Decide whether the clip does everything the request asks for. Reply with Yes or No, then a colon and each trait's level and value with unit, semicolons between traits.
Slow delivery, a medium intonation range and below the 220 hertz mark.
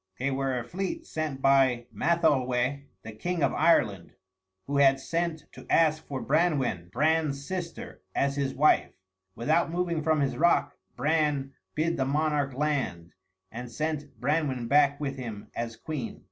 No: average, 150 wpm; average, 3.3 semitones; medium, 140 Hz